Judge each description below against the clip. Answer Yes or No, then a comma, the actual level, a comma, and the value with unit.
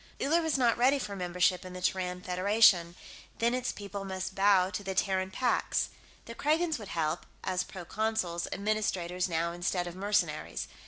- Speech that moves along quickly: No, average, 165 wpm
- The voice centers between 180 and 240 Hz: Yes, high, 190 Hz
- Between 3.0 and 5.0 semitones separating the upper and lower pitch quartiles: Yes, average, 3.3 semitones